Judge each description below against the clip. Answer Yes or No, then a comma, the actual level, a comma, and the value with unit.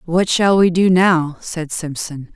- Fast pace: No, average, 180 wpm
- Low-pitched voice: No, medium, 170 Hz